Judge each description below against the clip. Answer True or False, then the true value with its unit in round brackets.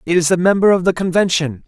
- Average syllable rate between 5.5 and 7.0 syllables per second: True (6.5 syllables/s)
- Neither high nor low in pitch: True (175 Hz)